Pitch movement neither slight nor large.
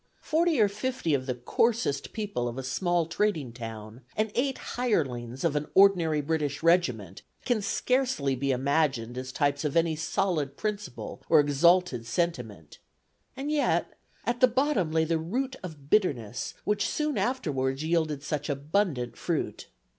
No: wide, 7.6 semitones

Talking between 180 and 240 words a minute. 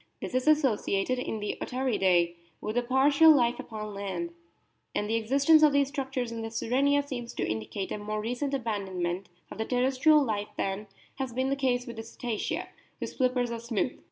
Yes: average, 190 wpm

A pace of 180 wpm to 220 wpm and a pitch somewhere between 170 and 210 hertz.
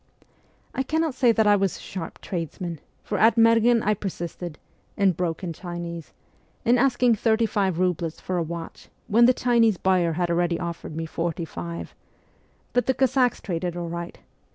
No: average, 170 wpm; medium, 185 Hz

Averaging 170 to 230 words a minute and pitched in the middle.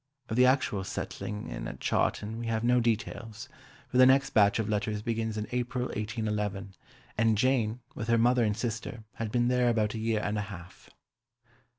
No: average, 190 wpm; low, 110 Hz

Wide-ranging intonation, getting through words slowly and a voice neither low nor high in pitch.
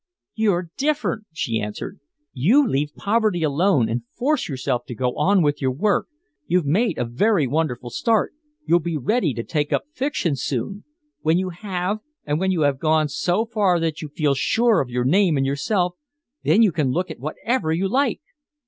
No: wide, 6.6 semitones; average, 190 wpm; medium, 165 Hz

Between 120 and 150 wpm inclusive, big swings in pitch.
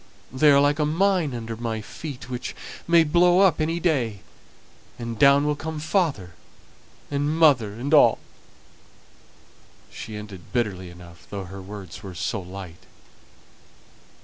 Yes: average, 140 wpm; wide, 7.4 semitones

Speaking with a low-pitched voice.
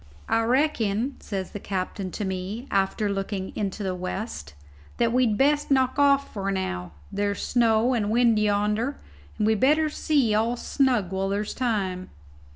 No: high, 215 Hz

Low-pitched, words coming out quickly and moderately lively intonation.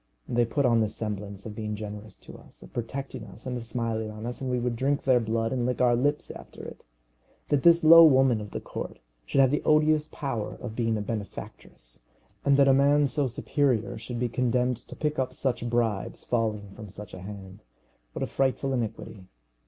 Yes: low, 120 Hz; fast, 210 wpm; average, 3.6 semitones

